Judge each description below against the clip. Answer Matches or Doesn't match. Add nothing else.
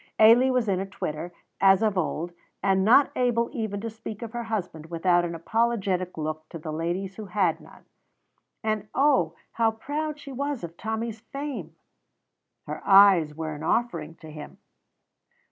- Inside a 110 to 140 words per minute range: Doesn't match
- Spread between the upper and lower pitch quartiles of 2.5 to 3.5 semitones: Doesn't match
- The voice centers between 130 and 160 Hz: Doesn't match